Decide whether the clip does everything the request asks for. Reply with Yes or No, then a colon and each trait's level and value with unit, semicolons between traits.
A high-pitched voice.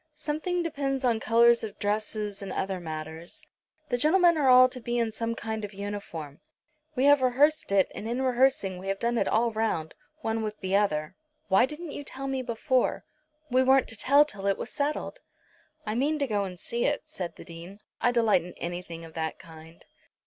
Yes: high, 225 Hz